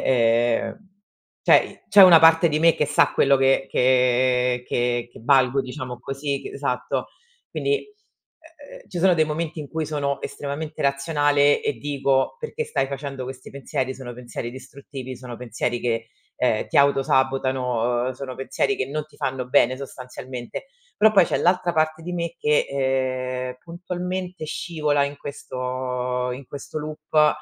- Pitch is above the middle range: No, low, 135 Hz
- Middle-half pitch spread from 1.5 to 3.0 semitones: No, average, 3.4 semitones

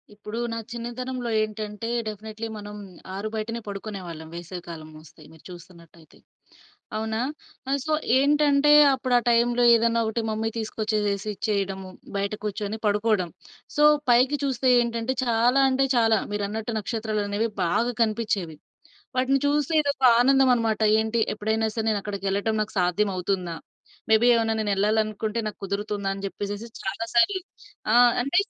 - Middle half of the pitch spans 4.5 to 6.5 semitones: No, average, 2.8 semitones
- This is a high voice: Yes, high, 220 Hz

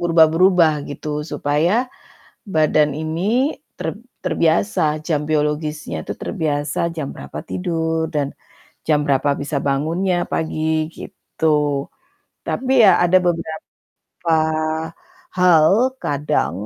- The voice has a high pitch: No, medium, 160 Hz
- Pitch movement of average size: No, narrow, 2.3 semitones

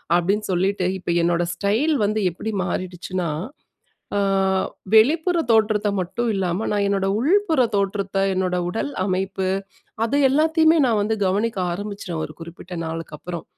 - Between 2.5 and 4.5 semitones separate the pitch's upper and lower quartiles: Yes, average, 4.0 semitones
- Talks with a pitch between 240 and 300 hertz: No, high, 200 Hz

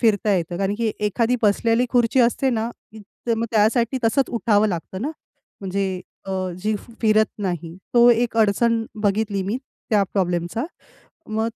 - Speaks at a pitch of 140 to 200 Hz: No, high, 220 Hz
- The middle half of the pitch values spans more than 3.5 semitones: No, average, 2.8 semitones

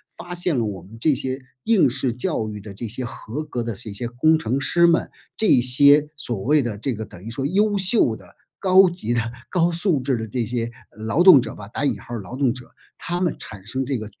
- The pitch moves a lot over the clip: Yes, wide, 6.1 semitones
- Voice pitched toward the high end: No, low, 130 Hz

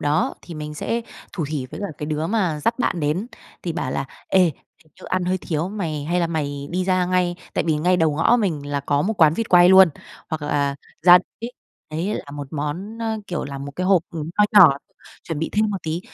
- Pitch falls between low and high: Yes, medium, 165 Hz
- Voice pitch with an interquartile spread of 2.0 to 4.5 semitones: Yes, average, 3.7 semitones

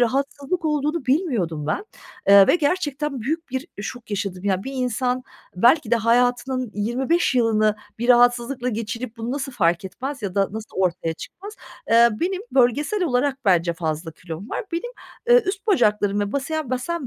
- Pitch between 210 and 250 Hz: Yes, high, 245 Hz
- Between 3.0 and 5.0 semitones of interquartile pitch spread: No, wide, 5.6 semitones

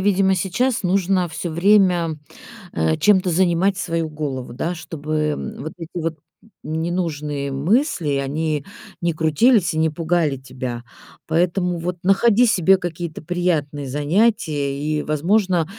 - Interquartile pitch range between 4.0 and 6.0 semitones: No, average, 3.5 semitones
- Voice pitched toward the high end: No, medium, 165 Hz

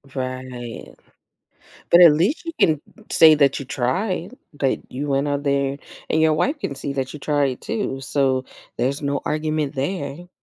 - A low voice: No, medium, 145 Hz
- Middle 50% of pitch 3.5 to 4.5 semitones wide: No, average, 2.9 semitones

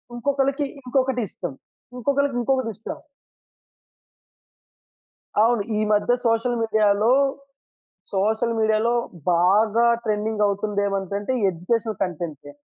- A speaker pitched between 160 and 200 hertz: No, high, 220 Hz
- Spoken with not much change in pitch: No, average, 3.1 semitones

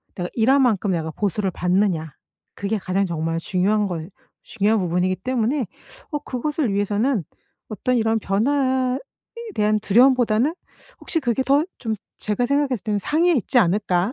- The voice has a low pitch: No, high, 215 Hz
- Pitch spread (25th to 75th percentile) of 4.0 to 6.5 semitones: Yes, average, 5.1 semitones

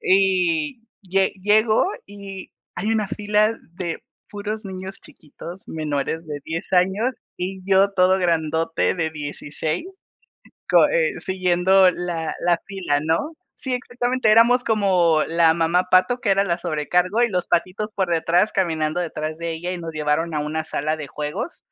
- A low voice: No, medium, 180 Hz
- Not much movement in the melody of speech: No, average, 3.7 semitones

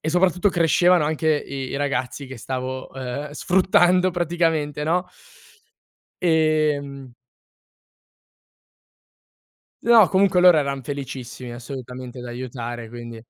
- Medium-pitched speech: Yes, medium, 145 Hz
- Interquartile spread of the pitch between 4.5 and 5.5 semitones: Yes, average, 5.2 semitones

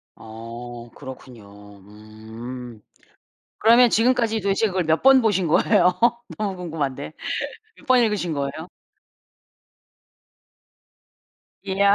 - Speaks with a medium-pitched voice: Yes, medium, 160 Hz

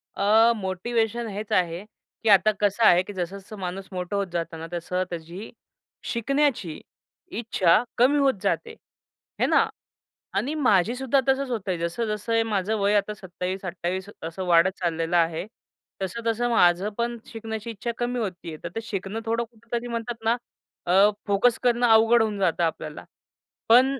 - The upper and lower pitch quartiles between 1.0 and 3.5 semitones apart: No, average, 4.4 semitones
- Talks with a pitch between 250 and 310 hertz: No, high, 205 Hz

